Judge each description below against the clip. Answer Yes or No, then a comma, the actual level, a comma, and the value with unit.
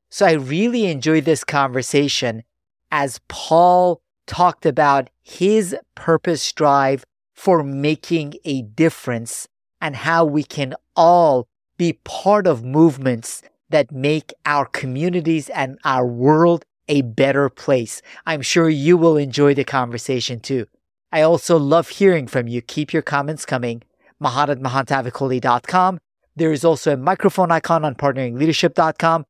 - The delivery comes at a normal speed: No, slow, 130 wpm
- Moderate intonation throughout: Yes, average, 3.7 semitones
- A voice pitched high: No, medium, 150 Hz